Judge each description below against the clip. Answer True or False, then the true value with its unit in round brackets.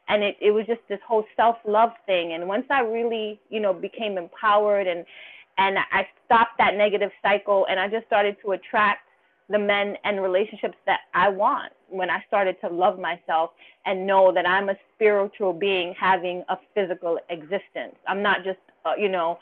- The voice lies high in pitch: True (200 Hz)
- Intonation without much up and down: True (2.2 semitones)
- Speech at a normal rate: True (190 wpm)